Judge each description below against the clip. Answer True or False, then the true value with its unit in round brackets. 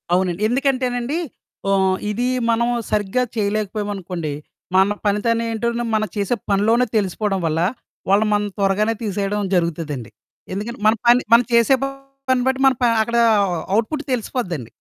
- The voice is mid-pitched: False (210 Hz)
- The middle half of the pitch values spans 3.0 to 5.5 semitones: True (3.5 semitones)